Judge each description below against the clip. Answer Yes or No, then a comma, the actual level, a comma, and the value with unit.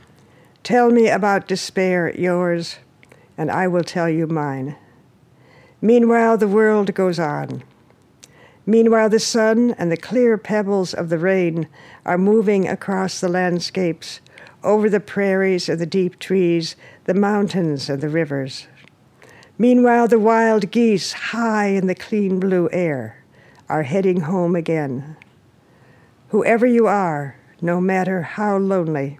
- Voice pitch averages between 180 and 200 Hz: Yes, medium, 185 Hz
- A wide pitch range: No, average, 4.3 semitones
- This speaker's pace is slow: Yes, slow, 130 wpm